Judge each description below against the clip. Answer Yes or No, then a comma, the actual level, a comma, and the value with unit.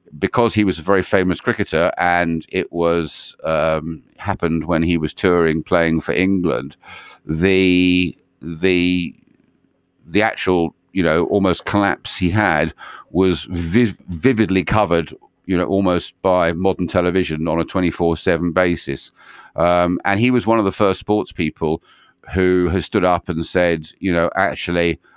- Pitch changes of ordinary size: No, narrow, 2.3 semitones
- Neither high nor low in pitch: No, very low, 90 Hz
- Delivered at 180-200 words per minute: No, average, 150 wpm